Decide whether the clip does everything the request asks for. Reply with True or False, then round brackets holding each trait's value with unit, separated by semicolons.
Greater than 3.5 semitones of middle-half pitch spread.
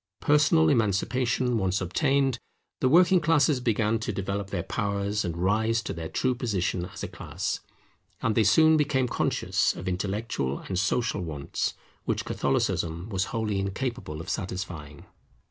True (5.2 semitones)